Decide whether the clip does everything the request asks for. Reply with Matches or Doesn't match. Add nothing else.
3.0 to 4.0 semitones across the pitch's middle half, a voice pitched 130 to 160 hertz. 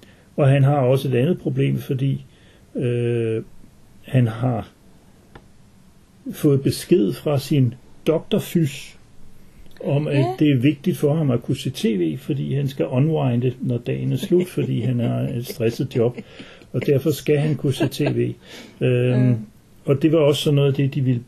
Matches